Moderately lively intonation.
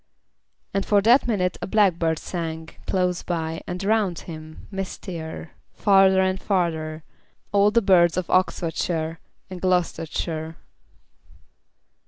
Yes: average, 3.0 semitones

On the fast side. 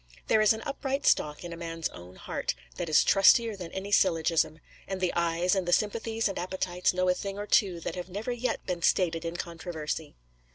Yes: fast, 210 wpm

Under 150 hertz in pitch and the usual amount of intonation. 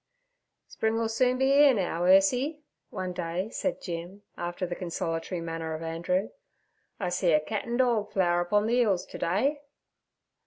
No: high, 190 Hz; average, 5.0 semitones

